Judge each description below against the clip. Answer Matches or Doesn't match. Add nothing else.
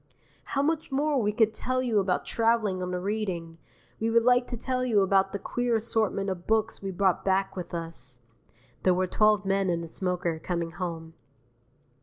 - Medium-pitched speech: Doesn't match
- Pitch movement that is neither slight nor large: Matches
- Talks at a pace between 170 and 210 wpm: Matches